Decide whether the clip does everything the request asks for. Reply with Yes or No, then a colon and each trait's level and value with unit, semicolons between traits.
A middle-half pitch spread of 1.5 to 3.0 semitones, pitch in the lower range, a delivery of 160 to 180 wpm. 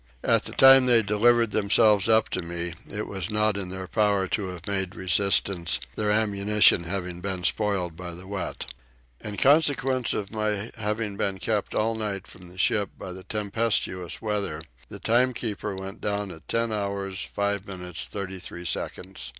Yes: narrow, 2.5 semitones; low, 100 Hz; average, 165 wpm